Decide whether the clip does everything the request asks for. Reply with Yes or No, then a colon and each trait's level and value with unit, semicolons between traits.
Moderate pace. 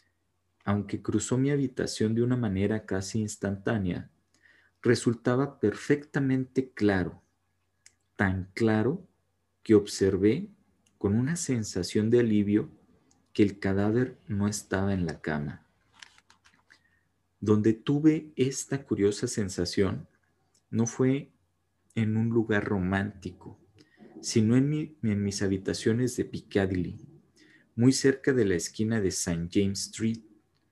No: slow, 110 wpm